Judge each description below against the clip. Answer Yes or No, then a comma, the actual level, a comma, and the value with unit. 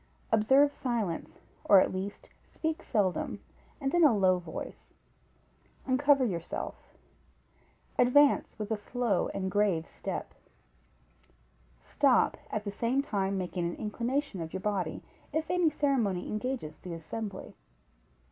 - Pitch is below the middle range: No, high, 215 Hz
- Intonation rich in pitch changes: Yes, wide, 6.2 semitones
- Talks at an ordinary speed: No, slow, 125 wpm